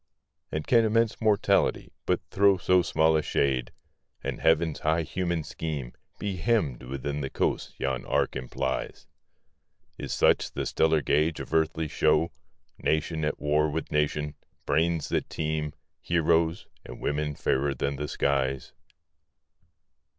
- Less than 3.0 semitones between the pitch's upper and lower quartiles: Yes, narrow, 2.5 semitones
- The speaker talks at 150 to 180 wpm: No, slow, 135 wpm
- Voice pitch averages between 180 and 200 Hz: No, very low, 80 Hz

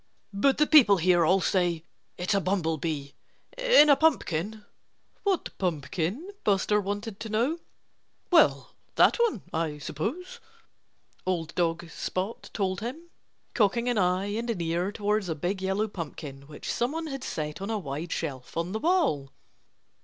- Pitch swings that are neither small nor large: No, wide, 5.9 semitones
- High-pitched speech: Yes, high, 195 Hz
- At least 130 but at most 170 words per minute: Yes, average, 150 wpm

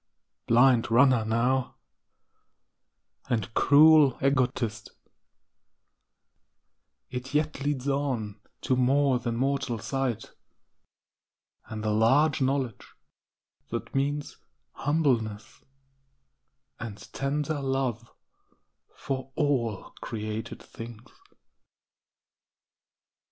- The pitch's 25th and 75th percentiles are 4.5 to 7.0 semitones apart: No, average, 3.3 semitones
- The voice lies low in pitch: Yes, low, 130 Hz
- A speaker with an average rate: No, slow, 75 wpm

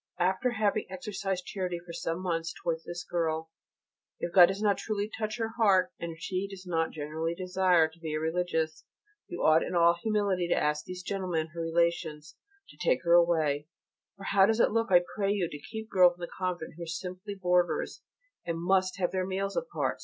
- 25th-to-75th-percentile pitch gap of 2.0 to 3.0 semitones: Yes, average, 2.7 semitones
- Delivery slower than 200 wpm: No, fast, 205 wpm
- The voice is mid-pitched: Yes, medium, 180 Hz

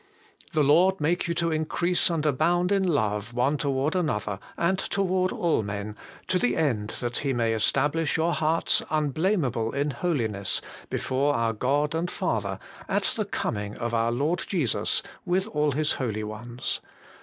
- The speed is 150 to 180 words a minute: Yes, average, 155 wpm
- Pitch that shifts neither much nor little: No, wide, 6.6 semitones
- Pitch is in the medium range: Yes, medium, 145 Hz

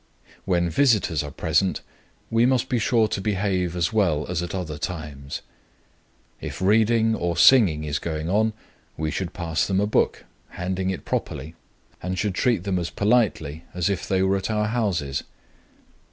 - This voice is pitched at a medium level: No, very low, 95 Hz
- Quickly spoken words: No, average, 165 wpm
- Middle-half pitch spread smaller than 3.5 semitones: No, average, 4.6 semitones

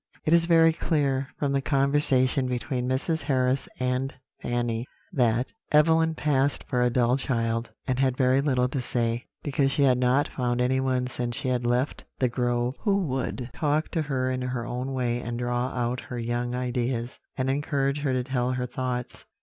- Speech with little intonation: Yes, narrow, 2.0 semitones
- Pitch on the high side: No, low, 130 Hz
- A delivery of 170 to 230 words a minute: Yes, average, 180 wpm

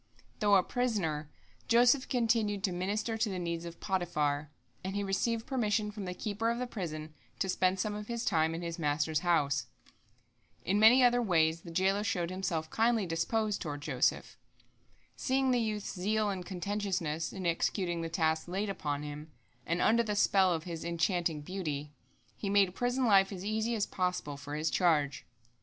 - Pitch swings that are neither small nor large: Yes, average, 4.5 semitones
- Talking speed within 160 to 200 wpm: Yes, average, 180 wpm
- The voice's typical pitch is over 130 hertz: Yes, medium, 185 Hz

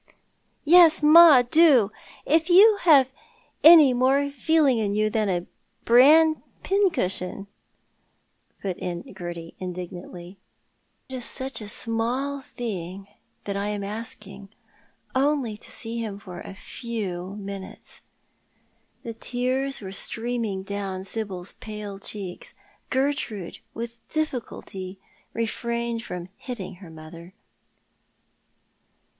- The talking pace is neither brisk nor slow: No, slow, 110 wpm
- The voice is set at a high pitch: Yes, high, 225 Hz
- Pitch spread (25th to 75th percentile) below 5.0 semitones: No, wide, 5.5 semitones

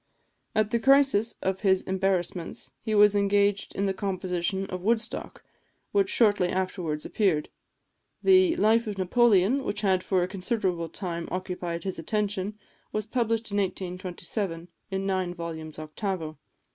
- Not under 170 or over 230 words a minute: No, average, 140 wpm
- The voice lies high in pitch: Yes, high, 195 Hz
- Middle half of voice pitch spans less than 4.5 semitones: Yes, average, 2.8 semitones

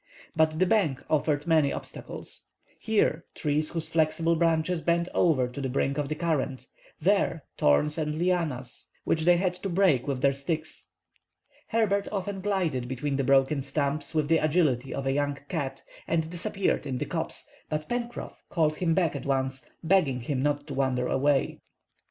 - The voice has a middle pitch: Yes, medium, 155 Hz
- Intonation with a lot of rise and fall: No, average, 3.7 semitones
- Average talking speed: Yes, average, 170 wpm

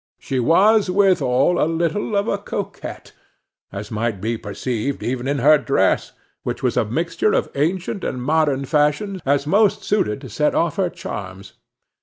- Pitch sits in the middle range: Yes, medium, 150 Hz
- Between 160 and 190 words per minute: Yes, average, 165 wpm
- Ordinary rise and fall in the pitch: No, wide, 6.9 semitones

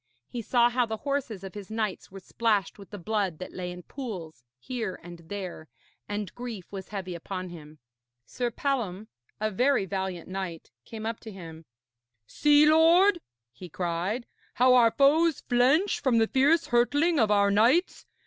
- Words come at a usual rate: Yes, average, 170 wpm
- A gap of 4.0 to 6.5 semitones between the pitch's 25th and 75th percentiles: Yes, wide, 5.4 semitones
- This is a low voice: No, high, 215 Hz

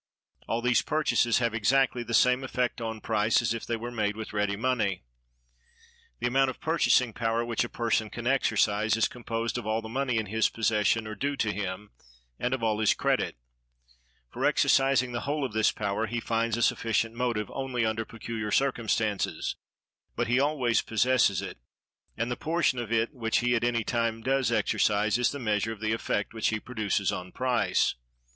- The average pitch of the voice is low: Yes, low, 115 Hz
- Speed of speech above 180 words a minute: Yes, average, 190 wpm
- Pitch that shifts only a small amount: Yes, narrow, 2.3 semitones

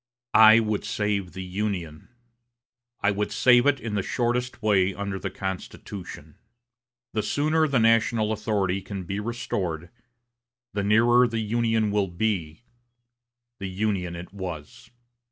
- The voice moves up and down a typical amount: Yes, average, 3.2 semitones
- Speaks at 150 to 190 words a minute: No, slow, 135 wpm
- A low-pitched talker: Yes, low, 105 Hz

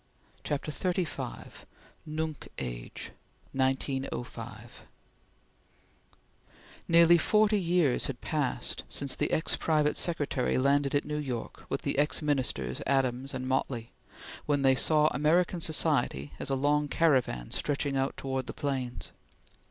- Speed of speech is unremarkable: No, slow, 120 wpm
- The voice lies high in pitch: No, medium, 140 Hz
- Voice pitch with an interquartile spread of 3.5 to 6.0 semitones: No, average, 2.9 semitones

